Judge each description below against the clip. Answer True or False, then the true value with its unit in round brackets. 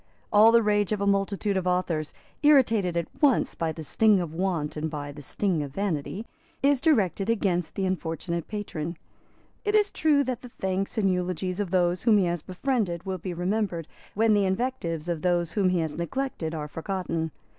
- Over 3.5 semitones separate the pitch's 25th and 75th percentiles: True (3.9 semitones)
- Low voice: False (185 Hz)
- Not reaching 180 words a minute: False (190 wpm)